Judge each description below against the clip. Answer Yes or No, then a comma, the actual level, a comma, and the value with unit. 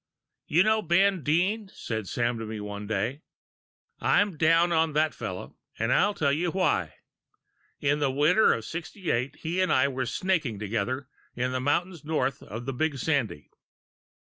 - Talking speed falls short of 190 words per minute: Yes, average, 165 wpm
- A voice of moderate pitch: Yes, medium, 145 Hz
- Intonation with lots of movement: Yes, wide, 6.3 semitones